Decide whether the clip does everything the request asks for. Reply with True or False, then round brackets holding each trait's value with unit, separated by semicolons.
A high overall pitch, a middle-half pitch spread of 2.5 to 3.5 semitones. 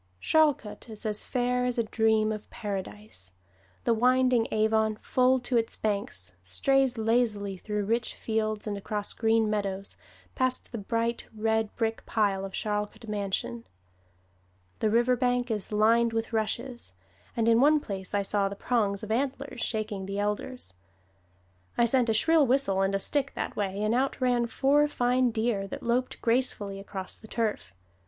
True (220 Hz; 3.0 semitones)